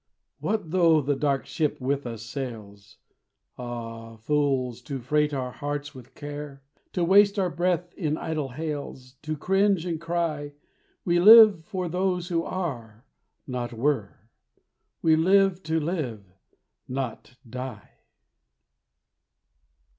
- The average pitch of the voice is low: No, medium, 145 Hz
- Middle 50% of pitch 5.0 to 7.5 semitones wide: Yes, average, 5.3 semitones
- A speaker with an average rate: No, slow, 125 wpm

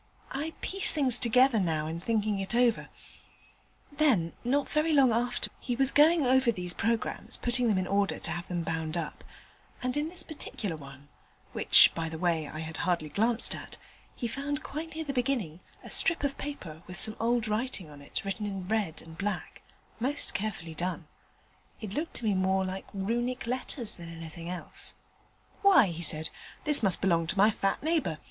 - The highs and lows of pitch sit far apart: Yes, wide, 7.0 semitones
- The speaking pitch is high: Yes, high, 215 Hz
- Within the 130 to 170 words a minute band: No, average, 185 wpm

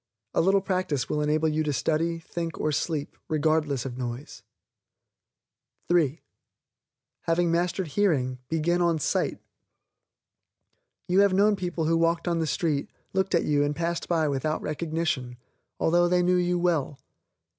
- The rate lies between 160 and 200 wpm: No, average, 145 wpm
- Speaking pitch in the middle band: Yes, medium, 165 Hz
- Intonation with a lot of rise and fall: No, average, 2.8 semitones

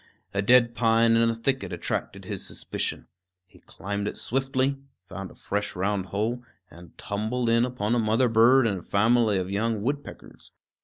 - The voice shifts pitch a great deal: No, average, 3.3 semitones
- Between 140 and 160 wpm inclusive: No, average, 170 wpm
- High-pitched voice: No, low, 115 Hz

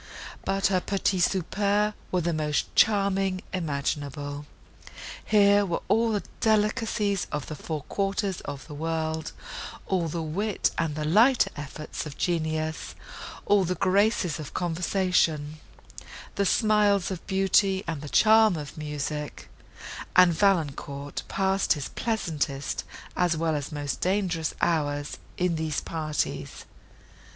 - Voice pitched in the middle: Yes, medium, 175 Hz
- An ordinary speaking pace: No, slow, 125 wpm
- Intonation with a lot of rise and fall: No, average, 4.5 semitones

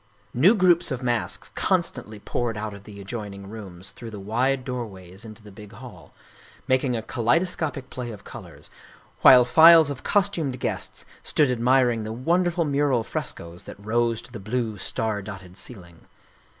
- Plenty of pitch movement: No, average, 4.1 semitones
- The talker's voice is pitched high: No, low, 120 Hz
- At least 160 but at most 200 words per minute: Yes, average, 165 wpm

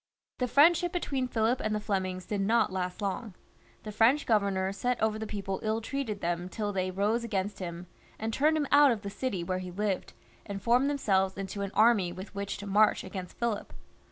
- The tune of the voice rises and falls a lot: No, average, 3.6 semitones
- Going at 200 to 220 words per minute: Yes, fast, 205 wpm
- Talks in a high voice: Yes, high, 210 Hz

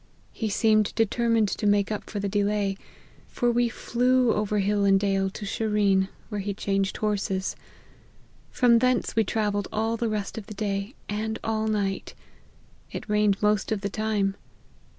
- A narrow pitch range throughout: Yes, narrow, 1.8 semitones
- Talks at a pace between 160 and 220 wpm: Yes, average, 165 wpm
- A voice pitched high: Yes, high, 210 Hz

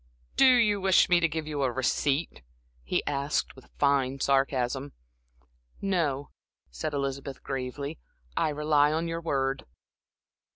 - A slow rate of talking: Yes, slow, 130 wpm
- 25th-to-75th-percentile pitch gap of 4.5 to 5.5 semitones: No, average, 3.1 semitones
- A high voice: No, medium, 145 Hz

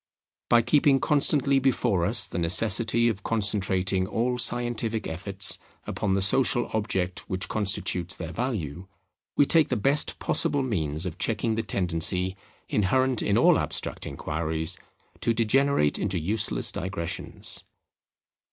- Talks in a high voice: No, low, 105 Hz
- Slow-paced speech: Yes, slow, 130 wpm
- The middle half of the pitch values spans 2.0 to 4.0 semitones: No, average, 4.8 semitones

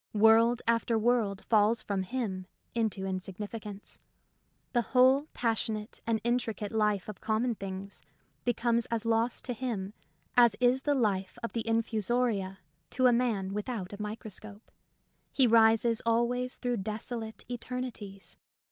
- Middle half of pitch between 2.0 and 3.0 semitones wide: Yes, narrow, 2.6 semitones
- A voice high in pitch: Yes, high, 225 Hz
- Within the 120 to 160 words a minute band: Yes, slow, 135 wpm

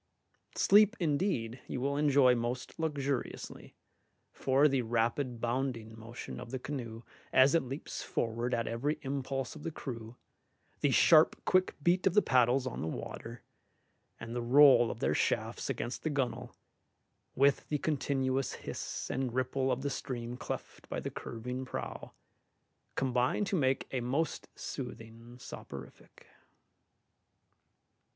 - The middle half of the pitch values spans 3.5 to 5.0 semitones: No, average, 3.0 semitones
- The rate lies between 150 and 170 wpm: No, average, 140 wpm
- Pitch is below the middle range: Yes, low, 130 Hz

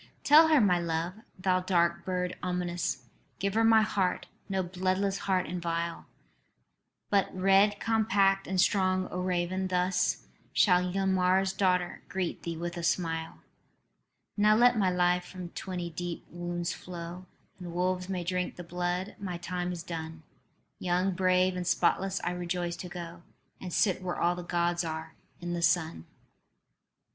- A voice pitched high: No, medium, 180 Hz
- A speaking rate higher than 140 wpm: Yes, average, 155 wpm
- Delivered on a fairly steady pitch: Yes, narrow, 1.5 semitones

